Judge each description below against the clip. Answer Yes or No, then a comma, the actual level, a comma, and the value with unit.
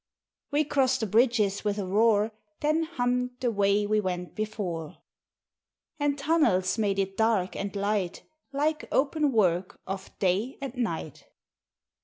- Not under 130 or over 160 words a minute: Yes, average, 140 wpm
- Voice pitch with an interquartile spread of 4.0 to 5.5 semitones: Yes, average, 5.1 semitones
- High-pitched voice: Yes, high, 215 Hz